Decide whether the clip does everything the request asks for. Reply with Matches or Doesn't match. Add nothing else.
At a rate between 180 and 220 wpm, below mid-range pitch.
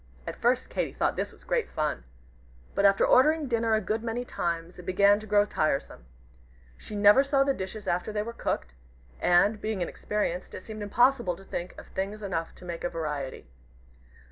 Doesn't match